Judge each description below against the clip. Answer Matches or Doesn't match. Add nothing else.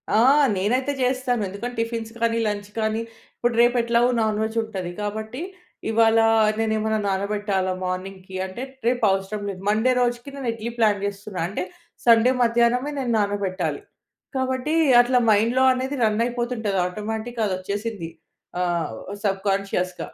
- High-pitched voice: Matches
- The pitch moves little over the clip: Doesn't match